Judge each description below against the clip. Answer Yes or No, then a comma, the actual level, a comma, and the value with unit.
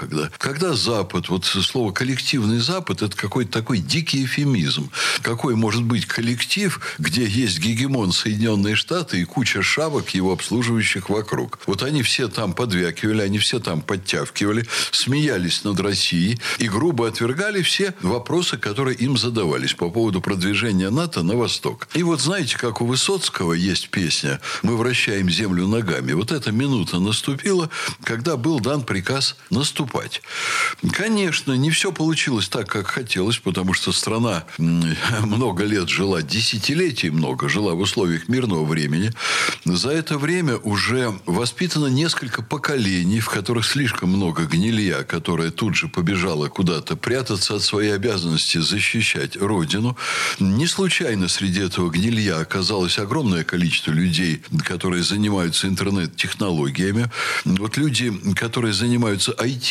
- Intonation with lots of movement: Yes, wide, 5.8 semitones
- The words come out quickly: No, average, 135 wpm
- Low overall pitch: Yes, low, 115 Hz